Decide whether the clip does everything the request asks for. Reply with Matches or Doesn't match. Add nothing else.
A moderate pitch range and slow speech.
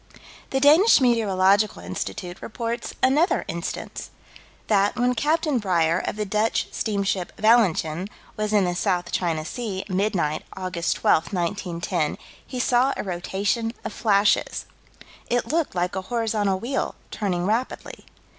Matches